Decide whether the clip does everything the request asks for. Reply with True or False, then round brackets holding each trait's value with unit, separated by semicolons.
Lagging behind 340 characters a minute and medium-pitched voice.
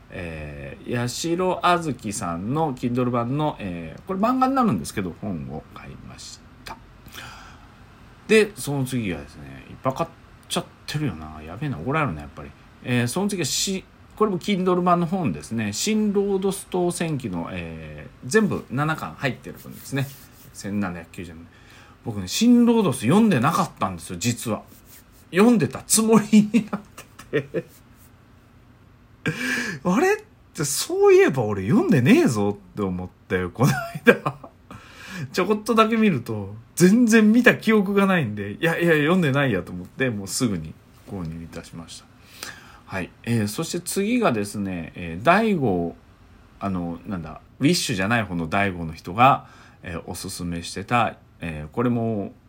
False (315 characters per minute; 120 Hz)